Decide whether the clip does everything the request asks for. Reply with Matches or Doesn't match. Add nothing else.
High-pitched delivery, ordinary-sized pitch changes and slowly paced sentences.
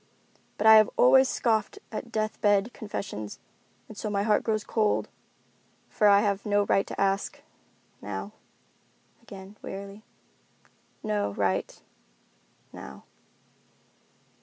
Doesn't match